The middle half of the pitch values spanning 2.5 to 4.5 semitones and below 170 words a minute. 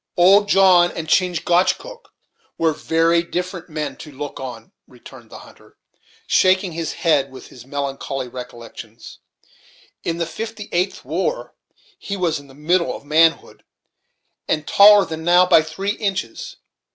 Yes: average, 4.1 semitones; average, 140 wpm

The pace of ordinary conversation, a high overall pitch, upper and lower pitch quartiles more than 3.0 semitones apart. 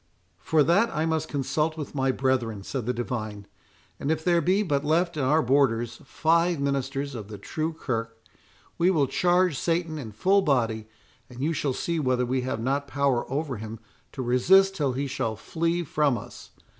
No: average, 185 wpm; medium, 140 Hz; average, 4.6 semitones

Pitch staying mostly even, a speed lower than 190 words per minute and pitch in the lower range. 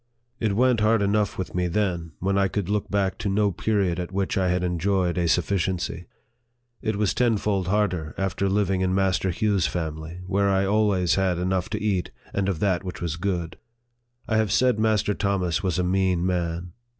No: narrow, 2.3 semitones; average, 195 wpm; very low, 95 Hz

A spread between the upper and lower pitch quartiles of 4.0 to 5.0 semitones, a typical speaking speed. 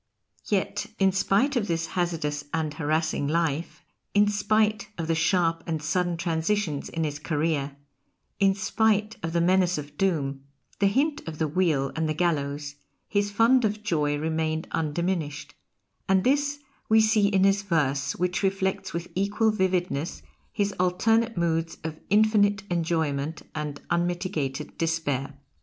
Yes: average, 4.5 semitones; average, 145 wpm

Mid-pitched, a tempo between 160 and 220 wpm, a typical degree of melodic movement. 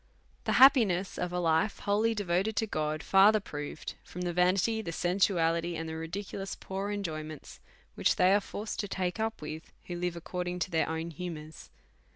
Yes: medium, 180 Hz; average, 180 wpm; average, 3.7 semitones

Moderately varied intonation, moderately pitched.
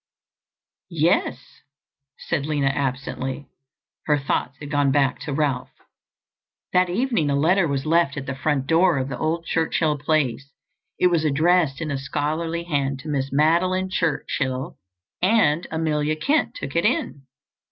Yes: average, 3.4 semitones; medium, 150 Hz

